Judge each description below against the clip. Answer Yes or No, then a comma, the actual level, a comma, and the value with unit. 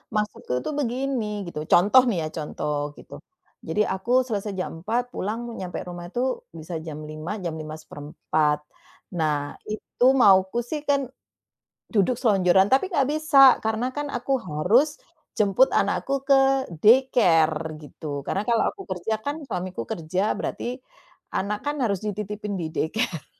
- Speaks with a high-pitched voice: Yes, high, 200 Hz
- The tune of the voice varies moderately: No, wide, 6.5 semitones